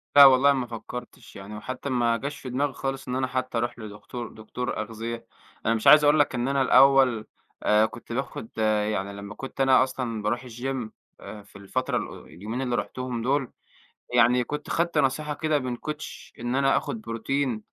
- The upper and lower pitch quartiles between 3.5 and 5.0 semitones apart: No, average, 3.1 semitones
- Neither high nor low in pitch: No, low, 125 Hz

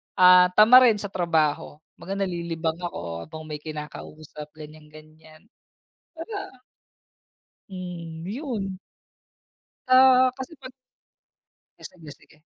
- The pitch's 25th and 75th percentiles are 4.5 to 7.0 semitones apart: Yes, wide, 5.4 semitones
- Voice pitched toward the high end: No, medium, 170 Hz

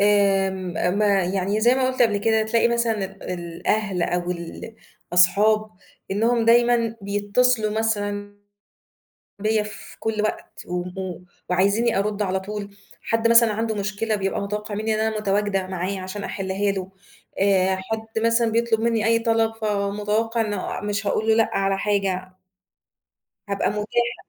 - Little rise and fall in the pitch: Yes, narrow, 2.3 semitones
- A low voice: No, high, 210 Hz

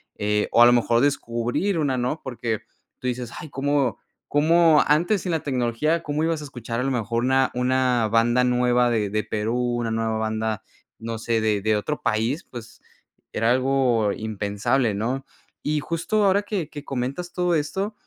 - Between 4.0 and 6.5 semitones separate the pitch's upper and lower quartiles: Yes, average, 4.7 semitones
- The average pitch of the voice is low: Yes, low, 125 Hz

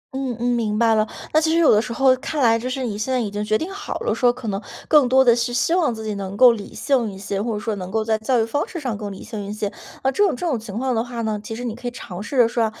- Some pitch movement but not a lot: Yes, average, 3.3 semitones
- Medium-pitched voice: No, high, 230 Hz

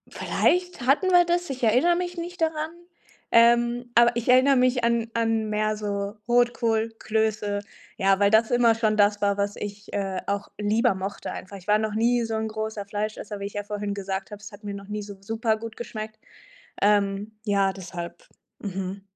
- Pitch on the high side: Yes, high, 215 Hz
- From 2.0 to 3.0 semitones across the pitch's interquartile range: Yes, average, 2.7 semitones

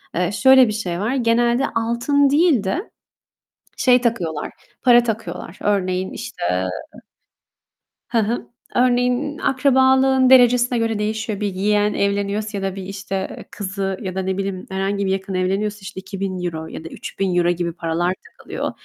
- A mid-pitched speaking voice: No, high, 205 Hz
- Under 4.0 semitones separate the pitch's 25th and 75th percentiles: No, average, 4.3 semitones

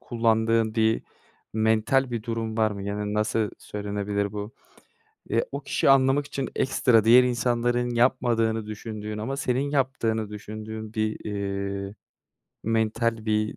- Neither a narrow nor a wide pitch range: No, narrow, 2.2 semitones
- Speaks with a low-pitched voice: Yes, low, 110 Hz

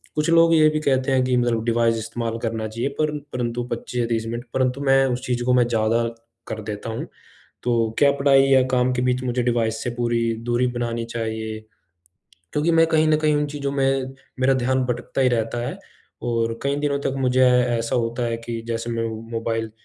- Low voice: Yes, low, 125 Hz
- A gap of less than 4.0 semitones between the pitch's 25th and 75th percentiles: Yes, average, 2.7 semitones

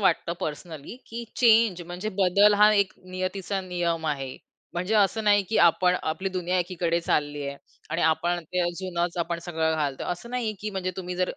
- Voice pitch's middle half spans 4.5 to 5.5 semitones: No, average, 3.0 semitones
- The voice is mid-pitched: Yes, medium, 180 Hz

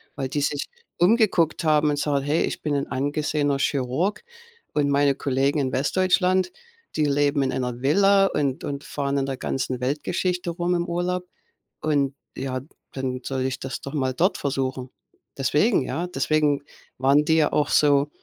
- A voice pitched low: No, medium, 145 Hz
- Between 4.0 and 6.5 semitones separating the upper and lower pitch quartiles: No, average, 3.2 semitones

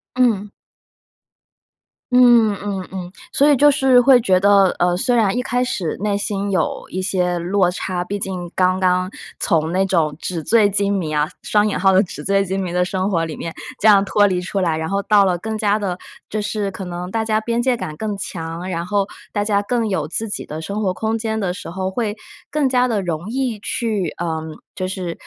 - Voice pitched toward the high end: Yes, high, 195 Hz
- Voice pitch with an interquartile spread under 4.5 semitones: Yes, average, 3.3 semitones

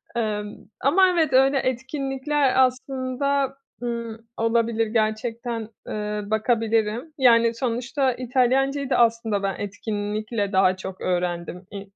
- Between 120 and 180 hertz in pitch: No, high, 235 Hz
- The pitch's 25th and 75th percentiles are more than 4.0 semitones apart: No, average, 3.7 semitones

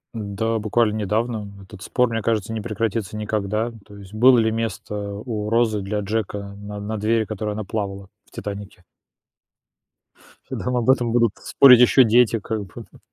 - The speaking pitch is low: Yes, low, 110 Hz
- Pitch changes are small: Yes, narrow, 1.9 semitones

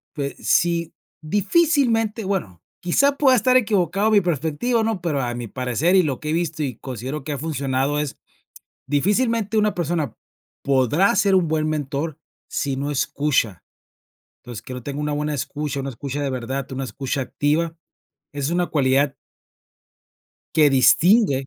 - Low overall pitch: No, medium, 150 Hz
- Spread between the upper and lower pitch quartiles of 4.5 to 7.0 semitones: Yes, wide, 5.5 semitones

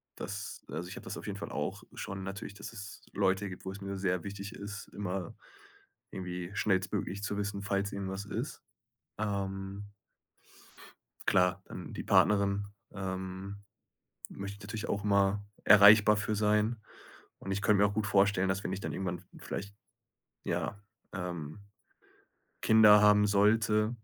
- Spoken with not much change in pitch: Yes, narrow, 1.3 semitones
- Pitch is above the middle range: No, low, 100 Hz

